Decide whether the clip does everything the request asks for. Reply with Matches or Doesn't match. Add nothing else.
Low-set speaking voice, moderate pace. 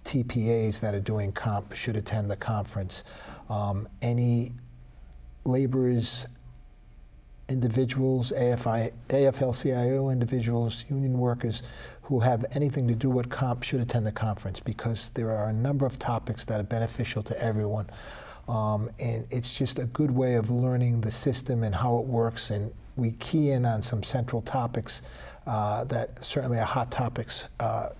Matches